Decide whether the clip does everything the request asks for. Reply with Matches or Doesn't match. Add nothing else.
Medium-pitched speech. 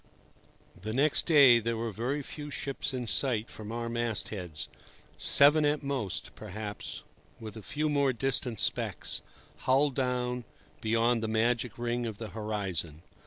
Doesn't match